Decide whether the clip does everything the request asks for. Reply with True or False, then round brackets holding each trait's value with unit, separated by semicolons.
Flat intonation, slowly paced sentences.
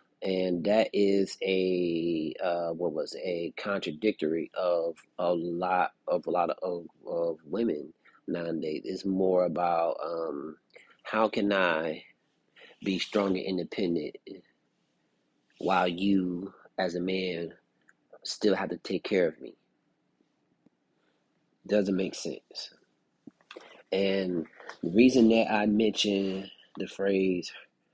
True (2.1 semitones; 120 wpm)